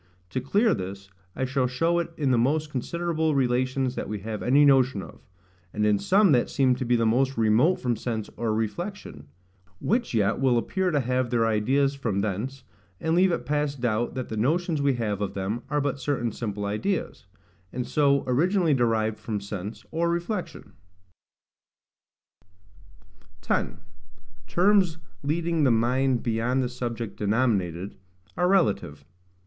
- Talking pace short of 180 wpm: Yes, average, 160 wpm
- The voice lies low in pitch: Yes, low, 125 Hz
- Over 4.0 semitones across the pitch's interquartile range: Yes, average, 5.3 semitones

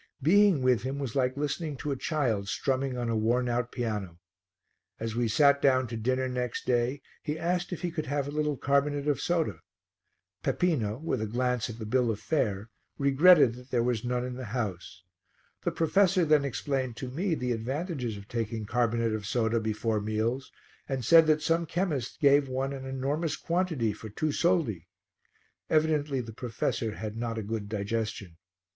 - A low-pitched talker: Yes, low, 130 Hz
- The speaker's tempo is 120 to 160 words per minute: No, average, 180 wpm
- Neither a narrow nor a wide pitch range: Yes, average, 4.6 semitones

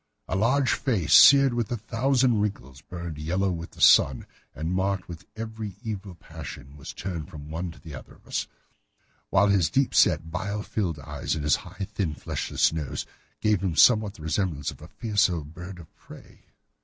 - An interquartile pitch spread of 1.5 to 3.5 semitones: No, average, 5.0 semitones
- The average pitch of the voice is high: No, very low, 95 Hz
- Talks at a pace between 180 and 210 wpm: Yes, average, 190 wpm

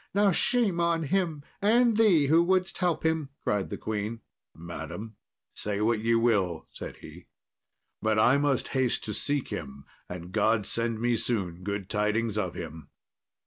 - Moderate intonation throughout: No, wide, 7.9 semitones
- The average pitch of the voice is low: Yes, low, 115 Hz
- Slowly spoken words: No, average, 160 wpm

